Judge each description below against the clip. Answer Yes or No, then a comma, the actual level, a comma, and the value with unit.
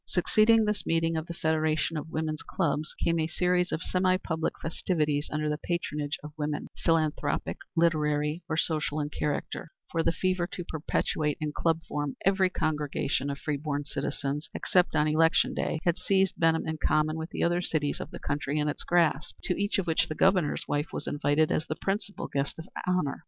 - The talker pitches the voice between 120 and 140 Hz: No, medium, 160 Hz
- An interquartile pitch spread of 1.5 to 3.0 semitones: Yes, narrow, 2.5 semitones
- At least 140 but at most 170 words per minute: No, average, 195 wpm